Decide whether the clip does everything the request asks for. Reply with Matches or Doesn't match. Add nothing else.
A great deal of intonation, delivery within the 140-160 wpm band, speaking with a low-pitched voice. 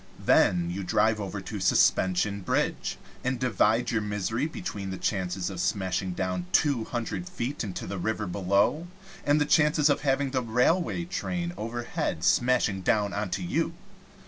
Matches